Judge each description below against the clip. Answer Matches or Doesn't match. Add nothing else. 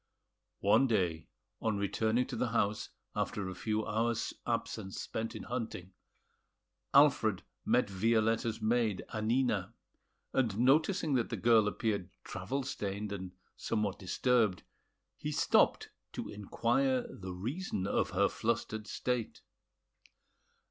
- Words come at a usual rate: Doesn't match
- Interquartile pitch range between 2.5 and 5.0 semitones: Matches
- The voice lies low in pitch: Matches